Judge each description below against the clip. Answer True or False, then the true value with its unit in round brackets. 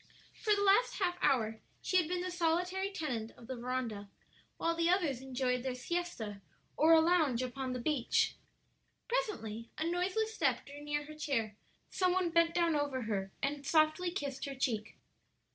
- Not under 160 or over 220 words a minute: True (175 wpm)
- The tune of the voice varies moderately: False (5.9 semitones)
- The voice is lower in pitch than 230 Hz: False (295 Hz)